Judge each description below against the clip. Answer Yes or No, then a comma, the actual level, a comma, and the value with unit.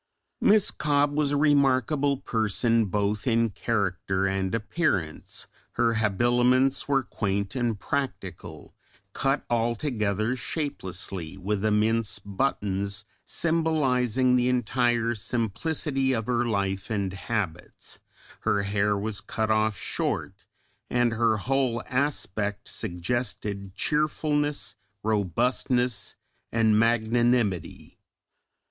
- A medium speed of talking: No, slow, 100 wpm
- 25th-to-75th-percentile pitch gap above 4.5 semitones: No, average, 4.2 semitones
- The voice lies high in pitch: No, low, 115 Hz